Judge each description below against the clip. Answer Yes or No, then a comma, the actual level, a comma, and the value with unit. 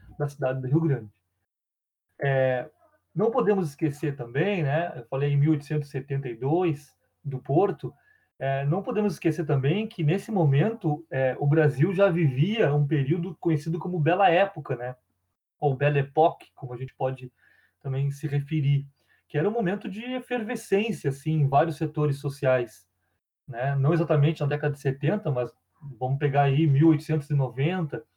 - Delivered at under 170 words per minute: Yes, average, 150 wpm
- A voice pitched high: No, medium, 150 Hz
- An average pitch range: Yes, average, 3.4 semitones